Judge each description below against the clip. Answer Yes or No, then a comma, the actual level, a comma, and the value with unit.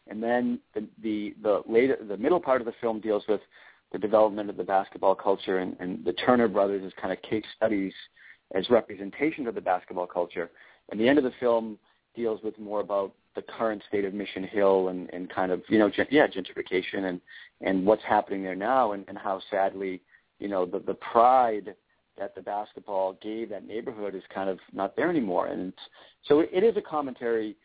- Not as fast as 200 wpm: No, fast, 205 wpm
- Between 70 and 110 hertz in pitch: Yes, low, 105 Hz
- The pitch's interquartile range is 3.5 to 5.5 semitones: No, average, 2.7 semitones